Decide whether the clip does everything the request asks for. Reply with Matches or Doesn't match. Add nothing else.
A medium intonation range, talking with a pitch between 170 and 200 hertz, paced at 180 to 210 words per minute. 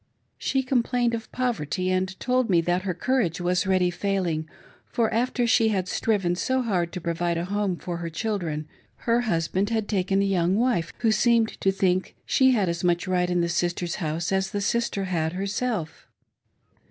Matches